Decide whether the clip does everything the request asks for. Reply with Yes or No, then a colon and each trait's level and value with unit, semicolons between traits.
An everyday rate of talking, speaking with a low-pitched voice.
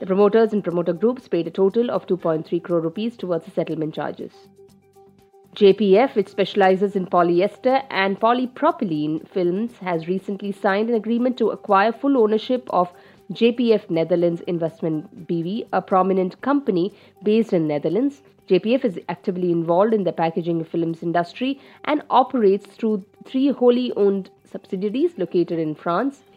No: average, 145 wpm; high, 195 Hz